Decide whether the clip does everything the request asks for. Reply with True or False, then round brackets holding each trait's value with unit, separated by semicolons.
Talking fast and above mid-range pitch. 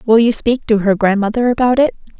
True (220 wpm; 225 Hz)